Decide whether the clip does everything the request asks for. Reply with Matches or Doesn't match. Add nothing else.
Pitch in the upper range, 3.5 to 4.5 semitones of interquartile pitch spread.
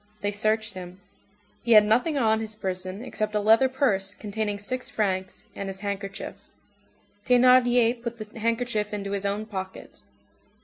Doesn't match